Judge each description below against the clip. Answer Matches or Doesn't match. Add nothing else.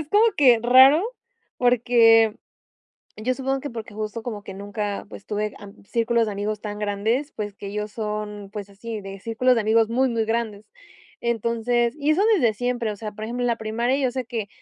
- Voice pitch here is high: Matches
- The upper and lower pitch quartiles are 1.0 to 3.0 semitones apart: Matches